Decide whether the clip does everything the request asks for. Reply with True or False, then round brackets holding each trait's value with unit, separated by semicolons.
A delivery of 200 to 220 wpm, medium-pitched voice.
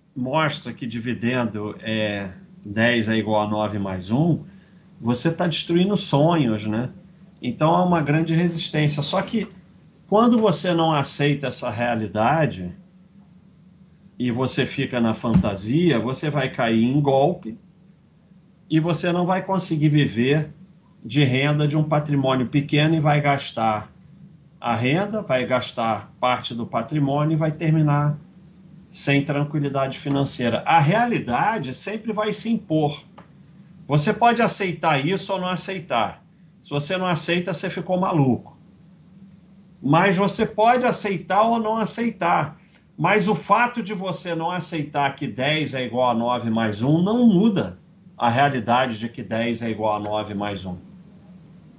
False (140 wpm; 160 Hz)